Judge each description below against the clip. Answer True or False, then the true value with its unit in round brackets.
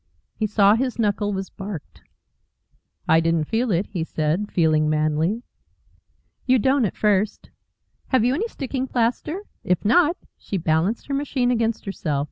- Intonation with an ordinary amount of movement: False (6.9 semitones)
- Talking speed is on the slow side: False (155 wpm)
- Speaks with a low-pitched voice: False (210 Hz)